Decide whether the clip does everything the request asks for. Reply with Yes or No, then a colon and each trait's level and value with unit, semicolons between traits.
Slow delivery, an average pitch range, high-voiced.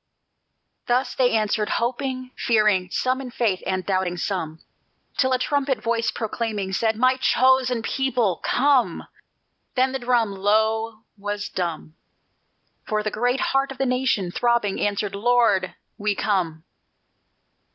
Yes: slow, 130 wpm; average, 4.0 semitones; high, 225 Hz